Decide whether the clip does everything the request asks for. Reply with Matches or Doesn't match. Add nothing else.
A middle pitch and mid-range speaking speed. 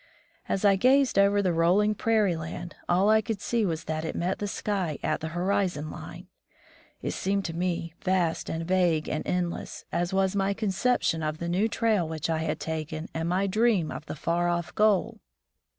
Matches